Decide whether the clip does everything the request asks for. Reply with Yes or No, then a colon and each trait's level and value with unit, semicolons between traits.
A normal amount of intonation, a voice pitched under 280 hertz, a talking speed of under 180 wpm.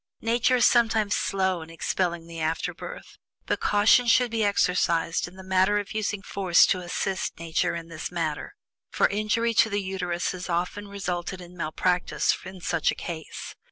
Yes: average, 3.2 semitones; medium, 185 Hz; average, 170 wpm